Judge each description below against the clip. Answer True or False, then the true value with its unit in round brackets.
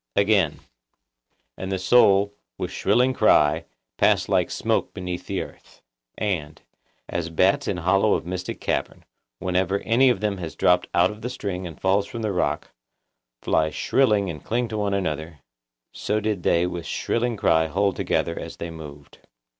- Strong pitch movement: False (3.8 semitones)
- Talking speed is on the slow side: False (165 wpm)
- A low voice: True (95 Hz)